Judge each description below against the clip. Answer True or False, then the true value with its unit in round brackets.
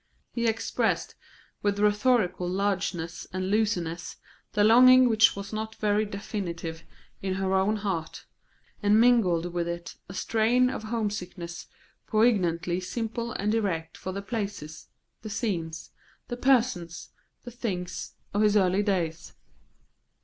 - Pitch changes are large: False (3.7 semitones)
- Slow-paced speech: True (130 wpm)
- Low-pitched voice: False (200 Hz)